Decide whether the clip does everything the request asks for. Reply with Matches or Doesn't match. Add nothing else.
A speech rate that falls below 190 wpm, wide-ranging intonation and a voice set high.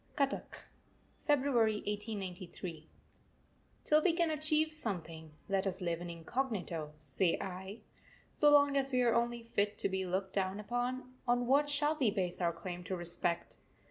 Matches